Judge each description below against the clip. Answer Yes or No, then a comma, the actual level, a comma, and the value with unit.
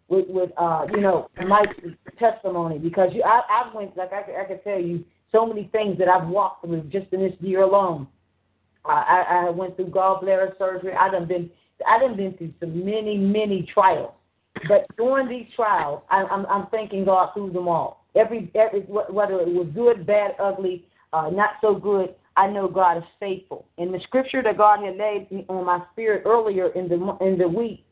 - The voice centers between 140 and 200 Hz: Yes, high, 190 Hz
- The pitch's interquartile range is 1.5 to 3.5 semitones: Yes, narrow, 2.5 semitones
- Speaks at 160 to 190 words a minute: No, average, 200 wpm